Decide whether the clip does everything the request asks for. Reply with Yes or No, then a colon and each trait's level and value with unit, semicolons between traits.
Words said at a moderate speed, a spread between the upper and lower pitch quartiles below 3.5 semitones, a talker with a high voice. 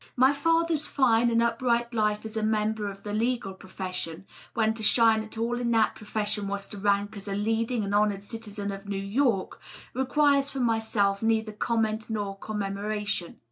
Yes: average, 180 wpm; narrow, 2.5 semitones; high, 220 Hz